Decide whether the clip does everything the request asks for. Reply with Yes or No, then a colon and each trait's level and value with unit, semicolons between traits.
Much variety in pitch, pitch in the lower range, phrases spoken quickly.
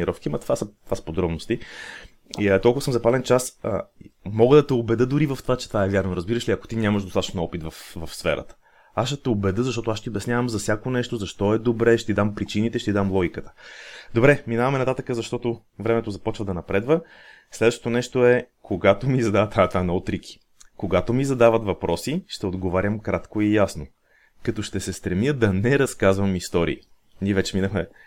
No: average, 3.8 semitones; low, 110 Hz; fast, 195 wpm